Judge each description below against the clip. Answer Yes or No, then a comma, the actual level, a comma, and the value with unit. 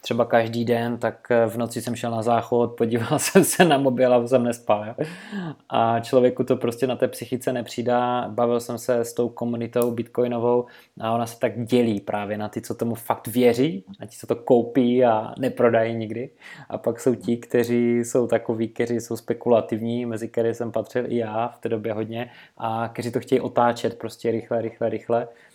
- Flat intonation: Yes, narrow, 1.1 semitones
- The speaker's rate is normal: No, fast, 195 wpm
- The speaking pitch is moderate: No, low, 120 Hz